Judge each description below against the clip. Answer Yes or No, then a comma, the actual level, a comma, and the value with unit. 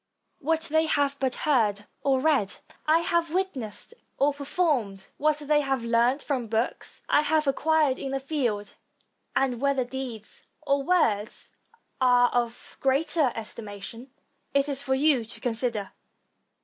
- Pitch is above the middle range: Yes, very high, 270 Hz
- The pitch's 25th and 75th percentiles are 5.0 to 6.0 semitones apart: No, average, 4.2 semitones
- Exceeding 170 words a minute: No, average, 145 wpm